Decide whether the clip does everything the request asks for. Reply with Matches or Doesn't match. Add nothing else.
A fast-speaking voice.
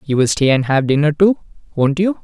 Matches